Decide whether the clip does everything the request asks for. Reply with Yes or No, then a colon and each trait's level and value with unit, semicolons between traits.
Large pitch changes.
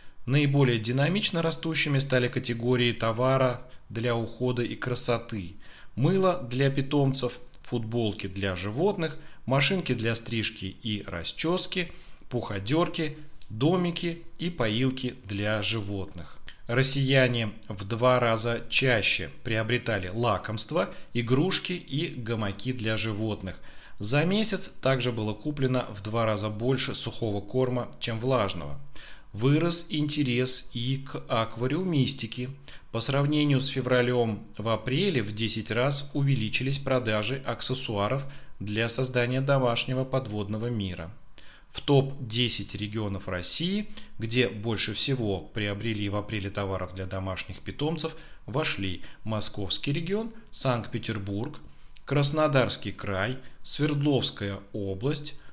No: average, 4.3 semitones